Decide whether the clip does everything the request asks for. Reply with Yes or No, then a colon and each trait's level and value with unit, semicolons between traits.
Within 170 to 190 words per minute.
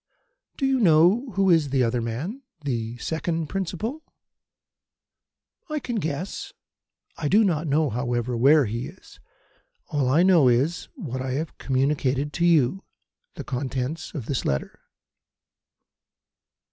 No: slow, 135 wpm